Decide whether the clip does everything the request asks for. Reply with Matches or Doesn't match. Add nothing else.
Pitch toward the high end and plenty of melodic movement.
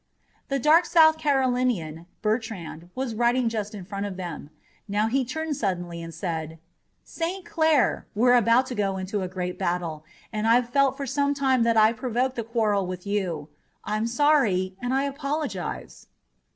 Matches